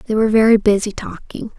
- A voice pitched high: Yes, high, 215 Hz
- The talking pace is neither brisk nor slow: Yes, average, 190 wpm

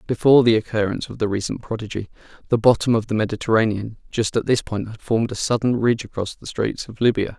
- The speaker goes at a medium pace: No, fast, 210 wpm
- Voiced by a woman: No, male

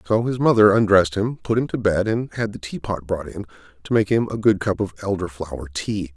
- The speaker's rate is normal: No, fast, 245 wpm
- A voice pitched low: Yes, low, 100 Hz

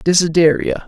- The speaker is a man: Yes, male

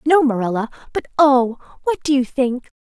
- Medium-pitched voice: No, very high, 265 Hz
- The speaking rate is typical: Yes, average, 165 wpm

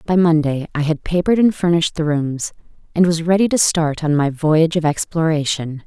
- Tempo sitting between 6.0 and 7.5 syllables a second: No, 5.5 syllables/s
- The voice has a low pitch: No, medium, 160 Hz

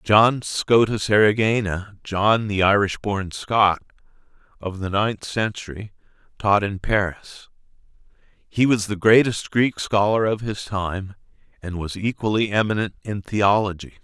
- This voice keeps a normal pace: No, slow, 130 wpm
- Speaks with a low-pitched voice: Yes, low, 105 Hz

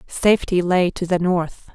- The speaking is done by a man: No, female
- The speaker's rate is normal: Yes, average, 170 wpm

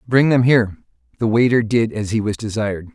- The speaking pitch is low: Yes, low, 115 Hz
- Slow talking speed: No, fast, 205 wpm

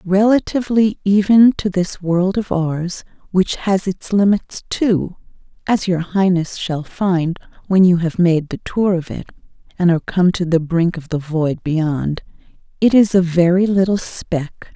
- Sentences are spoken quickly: No, average, 165 wpm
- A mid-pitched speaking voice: Yes, medium, 180 Hz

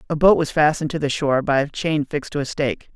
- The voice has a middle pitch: Yes, medium, 150 Hz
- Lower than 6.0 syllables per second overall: No, 6.9 syllables/s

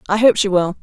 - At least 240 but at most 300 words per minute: Yes, fast, 290 wpm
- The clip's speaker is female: Yes, female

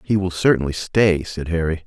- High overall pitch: No, very low, 90 Hz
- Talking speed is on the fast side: No, average, 195 wpm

